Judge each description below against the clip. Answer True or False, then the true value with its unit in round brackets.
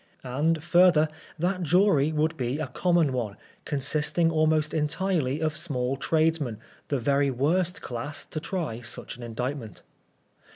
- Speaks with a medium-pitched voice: True (150 Hz)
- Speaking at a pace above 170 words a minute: False (135 wpm)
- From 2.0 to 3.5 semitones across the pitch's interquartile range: False (3.9 semitones)